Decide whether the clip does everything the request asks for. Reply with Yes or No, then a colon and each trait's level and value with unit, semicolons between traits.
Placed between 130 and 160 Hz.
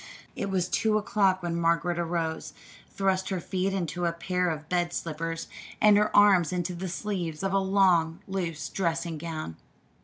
No: medium, 175 Hz